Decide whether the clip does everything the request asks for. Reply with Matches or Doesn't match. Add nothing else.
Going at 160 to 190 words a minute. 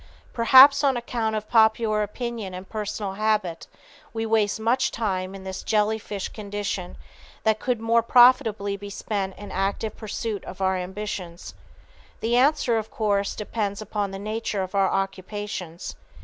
Doesn't match